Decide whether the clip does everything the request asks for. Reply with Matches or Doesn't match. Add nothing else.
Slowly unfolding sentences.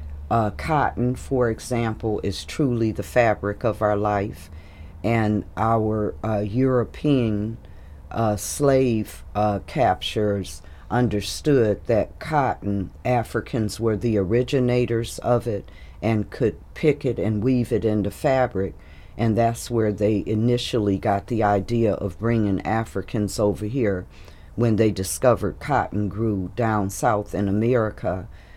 Matches